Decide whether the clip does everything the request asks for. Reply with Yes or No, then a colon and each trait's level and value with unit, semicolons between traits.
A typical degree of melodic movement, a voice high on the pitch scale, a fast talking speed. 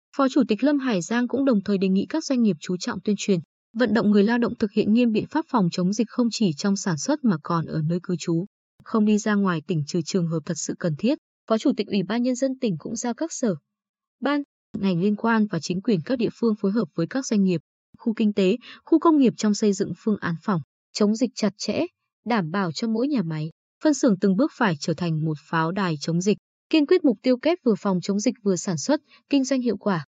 Yes: average, 4.9 semitones; high, 210 Hz; fast, 265 wpm